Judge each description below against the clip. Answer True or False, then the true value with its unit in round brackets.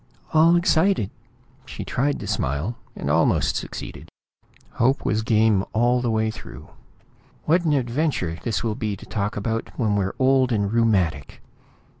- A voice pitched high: False (115 Hz)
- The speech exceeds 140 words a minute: True (150 wpm)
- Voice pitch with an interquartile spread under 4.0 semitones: False (4.6 semitones)